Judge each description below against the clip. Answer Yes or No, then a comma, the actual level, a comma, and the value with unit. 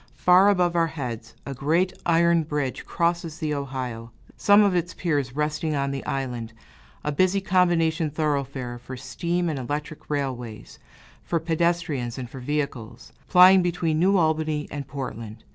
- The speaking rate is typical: Yes, average, 150 wpm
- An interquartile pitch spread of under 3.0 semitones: No, average, 4.4 semitones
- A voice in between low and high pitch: Yes, medium, 150 Hz